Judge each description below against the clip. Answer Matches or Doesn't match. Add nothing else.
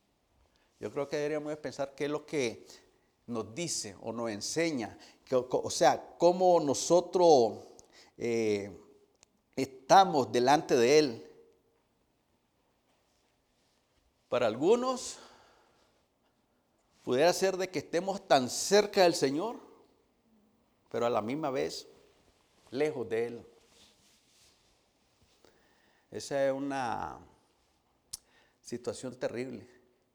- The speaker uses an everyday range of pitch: Doesn't match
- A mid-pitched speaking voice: Matches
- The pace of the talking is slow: Matches